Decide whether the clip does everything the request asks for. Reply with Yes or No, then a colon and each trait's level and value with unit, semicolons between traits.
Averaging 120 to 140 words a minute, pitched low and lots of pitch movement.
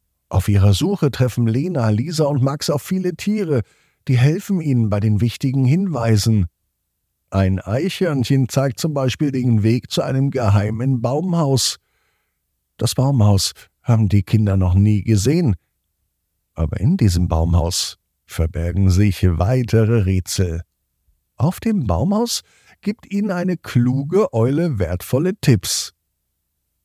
Yes: slow, 125 wpm; low, 115 Hz; wide, 7.4 semitones